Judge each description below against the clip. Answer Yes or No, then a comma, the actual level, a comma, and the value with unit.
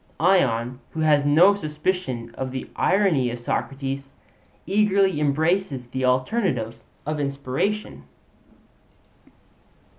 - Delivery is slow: Yes, slow, 95 wpm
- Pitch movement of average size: No, wide, 6.3 semitones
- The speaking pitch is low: No, medium, 145 Hz